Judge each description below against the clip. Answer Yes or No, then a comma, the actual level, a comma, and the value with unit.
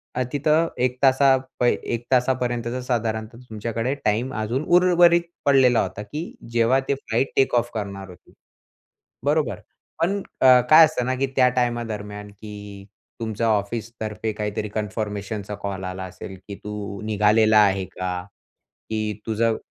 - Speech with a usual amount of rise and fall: Yes, average, 3.6 semitones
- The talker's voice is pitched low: Yes, low, 115 Hz